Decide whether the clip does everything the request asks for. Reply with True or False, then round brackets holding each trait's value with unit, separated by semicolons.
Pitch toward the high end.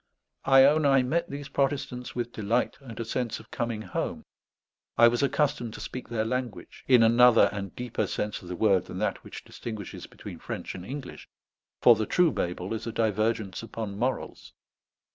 False (115 Hz)